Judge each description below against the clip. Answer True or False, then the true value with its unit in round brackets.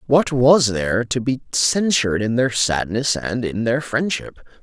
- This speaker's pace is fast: False (170 wpm)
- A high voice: False (125 Hz)